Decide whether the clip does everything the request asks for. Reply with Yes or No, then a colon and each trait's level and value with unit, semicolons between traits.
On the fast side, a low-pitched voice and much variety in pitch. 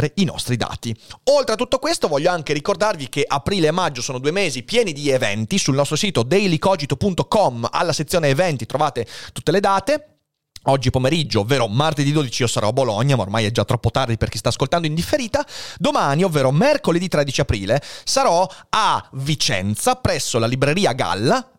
No: fast, 180 wpm; medium, 150 Hz; wide, 6.8 semitones